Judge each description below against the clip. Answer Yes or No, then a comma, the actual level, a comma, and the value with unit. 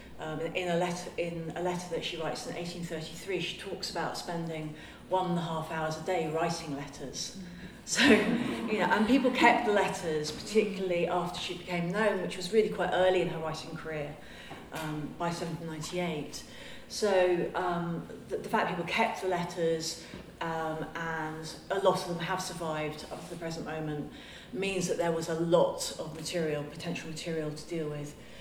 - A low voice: No, medium, 170 Hz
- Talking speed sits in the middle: Yes, average, 180 wpm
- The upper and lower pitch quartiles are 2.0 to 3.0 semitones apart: Yes, narrow, 2.4 semitones